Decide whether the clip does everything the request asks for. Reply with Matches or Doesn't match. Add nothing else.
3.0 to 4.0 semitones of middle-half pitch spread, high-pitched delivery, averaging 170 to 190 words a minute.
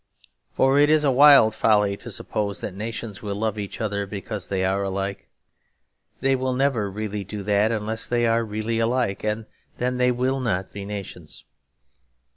Doesn't match